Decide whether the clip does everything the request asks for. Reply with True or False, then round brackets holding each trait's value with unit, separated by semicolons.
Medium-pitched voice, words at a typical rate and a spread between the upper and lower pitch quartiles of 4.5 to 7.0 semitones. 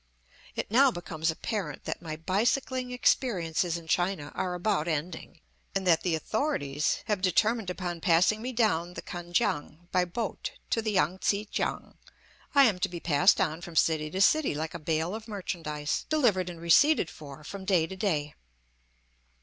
True (180 Hz; 175 wpm; 4.8 semitones)